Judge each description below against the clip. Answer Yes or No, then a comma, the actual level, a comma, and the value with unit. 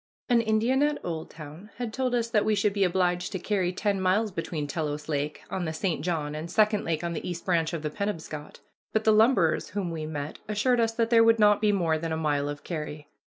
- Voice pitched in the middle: Yes, medium, 180 Hz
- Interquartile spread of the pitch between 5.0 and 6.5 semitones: Yes, average, 5.3 semitones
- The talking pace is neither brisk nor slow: No, fast, 235 wpm